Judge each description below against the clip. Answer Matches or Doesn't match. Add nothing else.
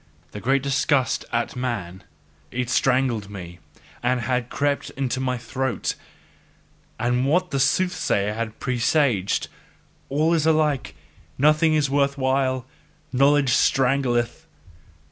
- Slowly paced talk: Matches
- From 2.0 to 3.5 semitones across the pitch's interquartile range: Matches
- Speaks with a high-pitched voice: Doesn't match